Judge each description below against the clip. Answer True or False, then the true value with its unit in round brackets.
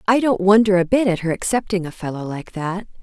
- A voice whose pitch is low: False (195 Hz)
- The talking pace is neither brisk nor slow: False (240 wpm)